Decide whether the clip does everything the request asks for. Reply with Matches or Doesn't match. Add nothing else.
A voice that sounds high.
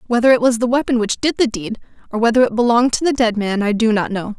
Matches